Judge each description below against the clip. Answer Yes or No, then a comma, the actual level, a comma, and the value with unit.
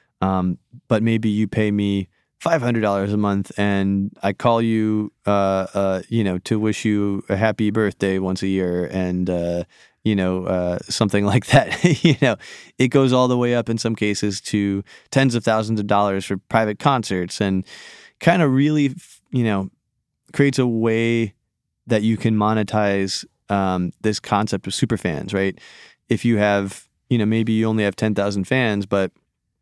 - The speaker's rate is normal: Yes, average, 180 wpm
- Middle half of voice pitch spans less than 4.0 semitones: Yes, average, 2.9 semitones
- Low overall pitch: Yes, low, 105 Hz